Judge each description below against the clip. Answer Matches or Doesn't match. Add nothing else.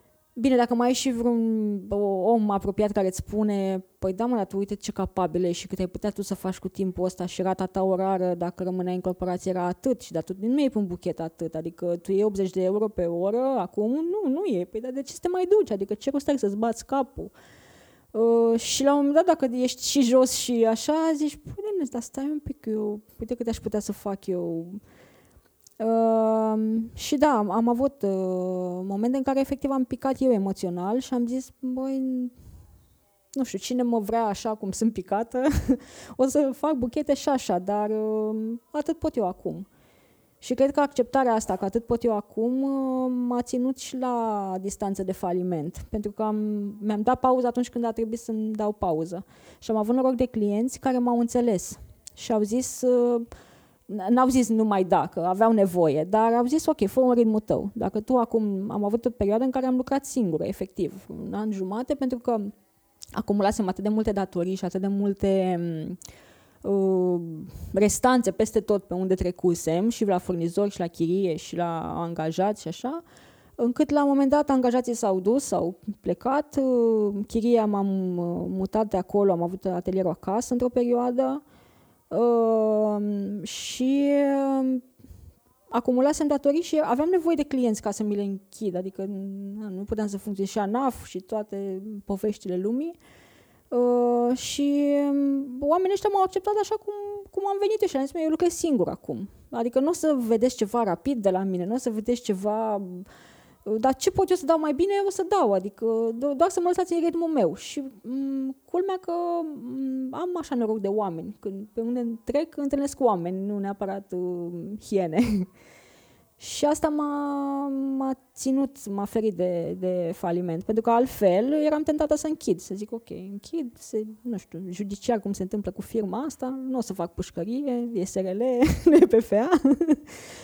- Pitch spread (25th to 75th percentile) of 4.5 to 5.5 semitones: Matches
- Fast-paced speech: Matches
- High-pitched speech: Matches